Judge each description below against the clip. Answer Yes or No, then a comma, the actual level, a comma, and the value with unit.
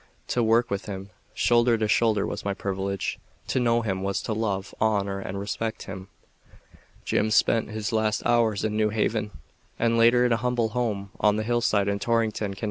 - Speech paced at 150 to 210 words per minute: Yes, average, 190 wpm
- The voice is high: No, low, 110 Hz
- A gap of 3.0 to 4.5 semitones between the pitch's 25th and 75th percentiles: No, narrow, 2.6 semitones